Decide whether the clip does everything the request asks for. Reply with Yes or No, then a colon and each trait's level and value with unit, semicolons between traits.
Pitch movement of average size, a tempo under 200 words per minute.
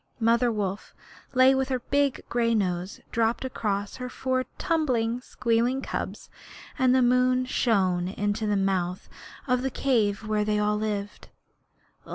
Yes: average, 3.7 semitones; average, 145 wpm